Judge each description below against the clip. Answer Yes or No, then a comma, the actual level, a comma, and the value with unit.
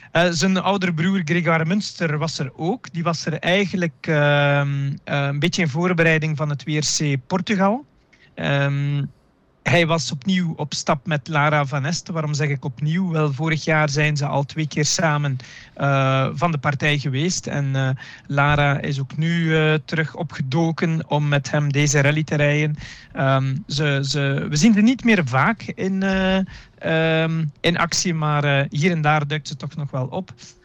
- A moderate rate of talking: Yes, average, 180 wpm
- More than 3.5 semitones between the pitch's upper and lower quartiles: No, average, 3.0 semitones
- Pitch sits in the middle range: Yes, medium, 155 Hz